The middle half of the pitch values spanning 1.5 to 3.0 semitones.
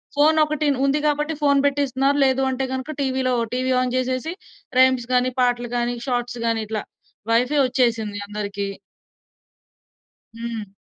Yes: average, 2.7 semitones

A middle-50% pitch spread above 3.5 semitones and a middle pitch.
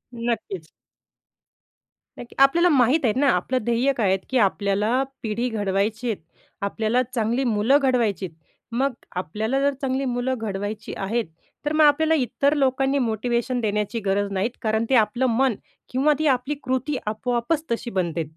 No: average, 3.9 semitones; high, 235 Hz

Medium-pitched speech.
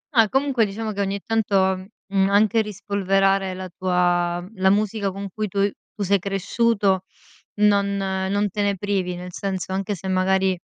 No: high, 195 Hz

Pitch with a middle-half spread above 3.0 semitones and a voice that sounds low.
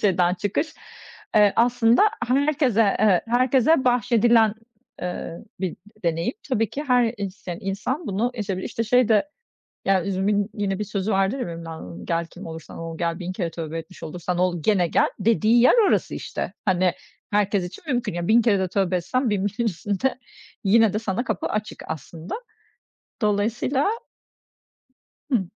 No: average, 4.6 semitones; high, 205 Hz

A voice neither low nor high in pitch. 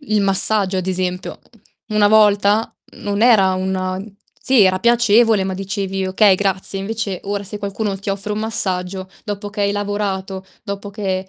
No: high, 200 Hz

